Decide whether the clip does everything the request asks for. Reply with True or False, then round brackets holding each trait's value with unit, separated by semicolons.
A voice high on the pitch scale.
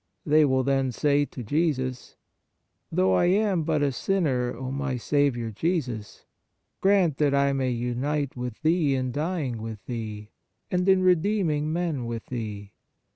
False (140 Hz)